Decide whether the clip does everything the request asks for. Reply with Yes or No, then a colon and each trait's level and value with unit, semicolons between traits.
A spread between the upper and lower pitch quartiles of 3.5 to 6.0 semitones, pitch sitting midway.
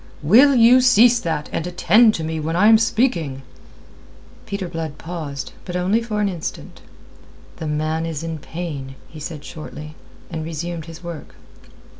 Yes: average, 5.1 semitones; medium, 165 Hz